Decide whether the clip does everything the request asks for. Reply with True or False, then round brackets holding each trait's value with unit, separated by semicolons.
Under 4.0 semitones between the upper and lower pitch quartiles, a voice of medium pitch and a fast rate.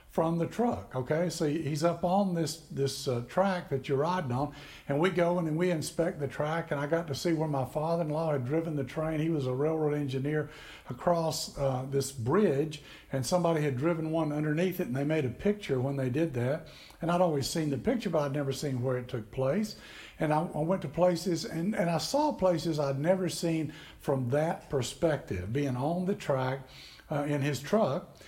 True (3.5 semitones; 155 Hz; 220 wpm)